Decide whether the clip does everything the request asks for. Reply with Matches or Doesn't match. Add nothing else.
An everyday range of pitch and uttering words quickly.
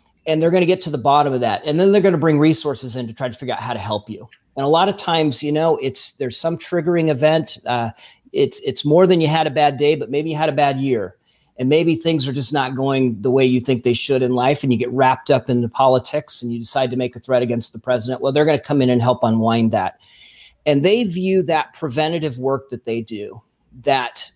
Matches